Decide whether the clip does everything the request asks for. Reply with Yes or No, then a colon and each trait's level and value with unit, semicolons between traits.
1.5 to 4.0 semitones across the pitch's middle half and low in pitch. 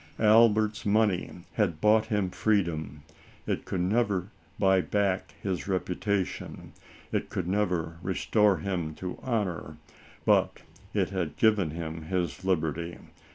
Yes: average, 3.4 semitones; very low, 95 Hz